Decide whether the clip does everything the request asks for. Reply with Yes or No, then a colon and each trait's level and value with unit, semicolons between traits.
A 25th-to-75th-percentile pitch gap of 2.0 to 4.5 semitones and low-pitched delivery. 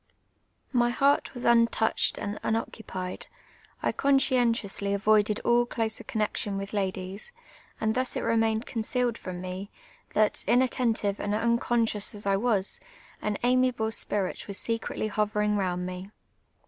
No: average, 3.0 semitones; high, 220 Hz